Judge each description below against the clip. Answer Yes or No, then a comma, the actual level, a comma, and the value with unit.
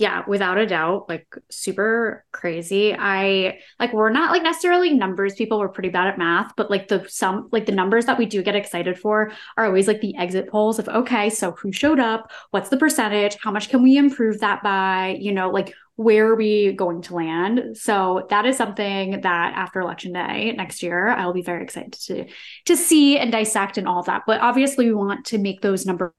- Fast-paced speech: Yes, fast, 220 wpm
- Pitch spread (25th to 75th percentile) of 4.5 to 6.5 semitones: No, average, 3.1 semitones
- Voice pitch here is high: Yes, high, 205 Hz